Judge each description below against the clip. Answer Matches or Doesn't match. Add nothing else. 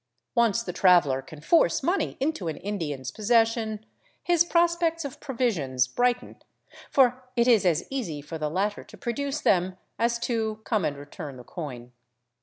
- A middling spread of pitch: Doesn't match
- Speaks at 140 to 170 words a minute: Matches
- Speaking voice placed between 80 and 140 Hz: Doesn't match